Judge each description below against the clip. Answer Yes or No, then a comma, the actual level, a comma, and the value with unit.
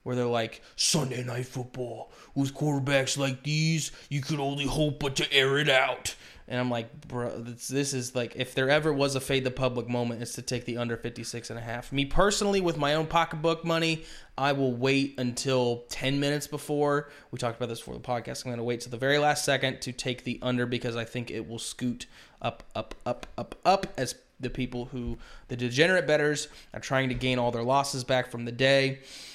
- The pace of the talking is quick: Yes, fast, 220 wpm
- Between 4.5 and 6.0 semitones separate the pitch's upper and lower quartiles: No, average, 2.8 semitones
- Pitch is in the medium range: No, low, 130 Hz